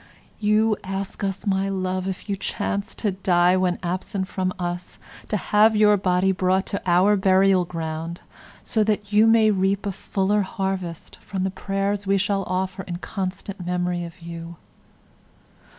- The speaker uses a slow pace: No, average, 160 wpm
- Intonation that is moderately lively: No, narrow, 1.8 semitones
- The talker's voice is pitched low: No, high, 190 Hz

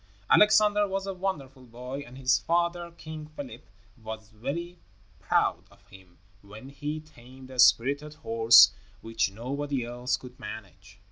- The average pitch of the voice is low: Yes, low, 130 Hz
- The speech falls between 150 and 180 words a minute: No, average, 140 wpm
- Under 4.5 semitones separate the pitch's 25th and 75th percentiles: No, wide, 5.6 semitones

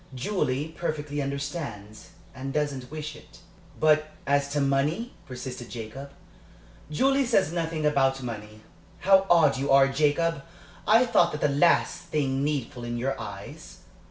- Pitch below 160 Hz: Yes, medium, 140 Hz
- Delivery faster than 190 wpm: No, average, 145 wpm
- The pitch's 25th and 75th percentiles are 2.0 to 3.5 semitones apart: Yes, average, 2.8 semitones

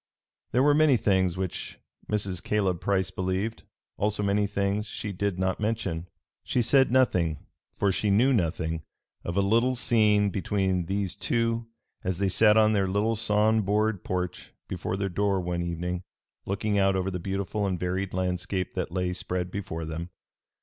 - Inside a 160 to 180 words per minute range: Yes, average, 165 wpm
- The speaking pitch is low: Yes, low, 100 Hz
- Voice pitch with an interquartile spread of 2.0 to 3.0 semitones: Yes, average, 2.7 semitones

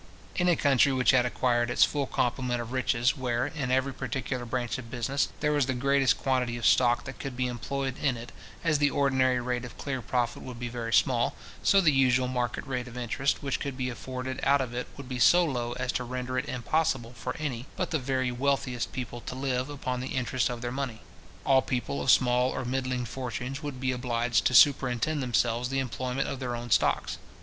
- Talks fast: Yes, fast, 215 wpm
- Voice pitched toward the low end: Yes, low, 130 Hz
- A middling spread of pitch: No, narrow, 1.7 semitones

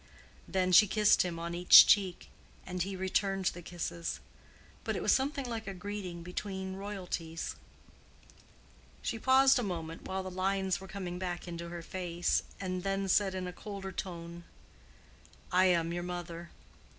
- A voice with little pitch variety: Yes, narrow, 2.0 semitones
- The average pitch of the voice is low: No, medium, 185 Hz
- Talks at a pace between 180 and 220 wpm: No, average, 160 wpm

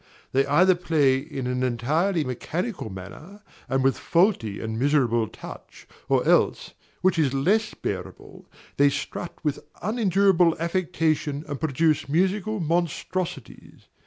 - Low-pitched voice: No, medium, 155 Hz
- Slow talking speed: Yes, slow, 125 wpm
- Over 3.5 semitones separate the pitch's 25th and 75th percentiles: Yes, wide, 5.4 semitones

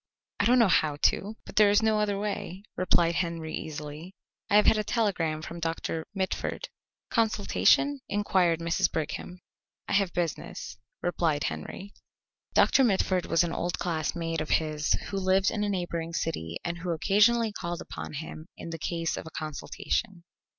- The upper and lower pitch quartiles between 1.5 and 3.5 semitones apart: No, average, 3.9 semitones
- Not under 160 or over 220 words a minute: Yes, average, 165 wpm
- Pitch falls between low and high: Yes, medium, 175 Hz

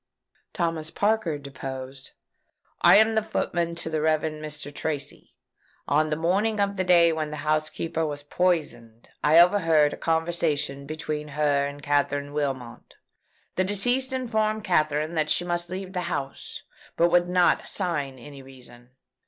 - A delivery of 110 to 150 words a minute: Yes, average, 145 wpm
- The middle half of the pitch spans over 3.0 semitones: Yes, average, 3.6 semitones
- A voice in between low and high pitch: Yes, medium, 155 Hz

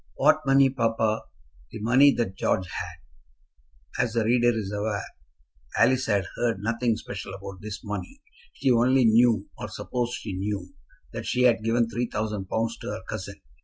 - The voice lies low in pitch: Yes, low, 110 Hz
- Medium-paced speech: Yes, average, 165 wpm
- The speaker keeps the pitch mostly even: No, average, 3.6 semitones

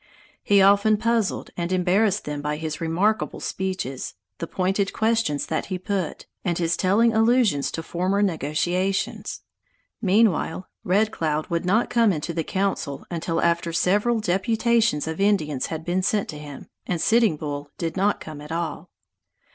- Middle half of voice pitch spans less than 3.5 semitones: No, average, 4.3 semitones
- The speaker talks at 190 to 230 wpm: No, average, 155 wpm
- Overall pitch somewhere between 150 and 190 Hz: Yes, medium, 185 Hz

